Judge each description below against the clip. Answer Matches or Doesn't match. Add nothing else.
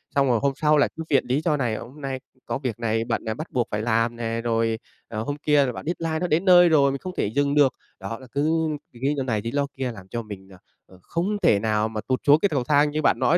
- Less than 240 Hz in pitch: Matches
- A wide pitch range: Doesn't match